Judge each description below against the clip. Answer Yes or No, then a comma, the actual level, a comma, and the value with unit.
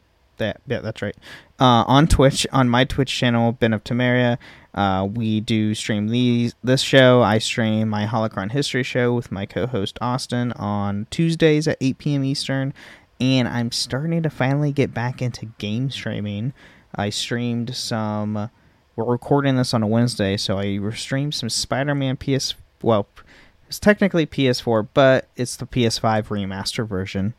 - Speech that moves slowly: No, average, 160 wpm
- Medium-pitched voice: No, low, 120 Hz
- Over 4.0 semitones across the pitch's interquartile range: No, average, 3.6 semitones